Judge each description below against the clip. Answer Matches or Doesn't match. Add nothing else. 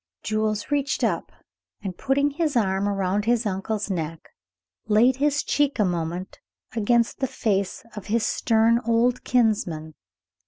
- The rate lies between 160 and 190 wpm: Doesn't match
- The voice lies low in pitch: Doesn't match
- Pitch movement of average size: Matches